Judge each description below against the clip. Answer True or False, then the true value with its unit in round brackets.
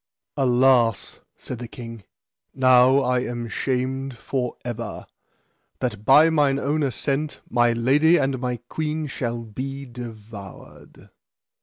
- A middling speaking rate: False (120 wpm)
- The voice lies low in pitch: True (125 Hz)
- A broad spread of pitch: False (2.5 semitones)